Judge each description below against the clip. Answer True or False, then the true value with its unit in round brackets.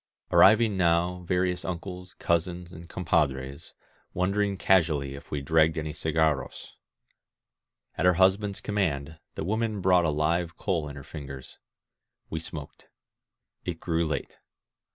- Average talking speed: False (130 wpm)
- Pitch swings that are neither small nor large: True (3.3 semitones)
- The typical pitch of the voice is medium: False (85 Hz)